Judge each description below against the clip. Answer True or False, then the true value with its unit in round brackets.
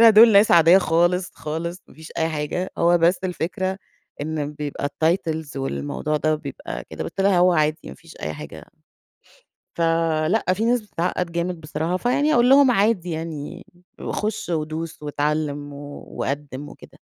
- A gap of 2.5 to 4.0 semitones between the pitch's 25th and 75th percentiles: True (3.5 semitones)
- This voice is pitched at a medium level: True (165 Hz)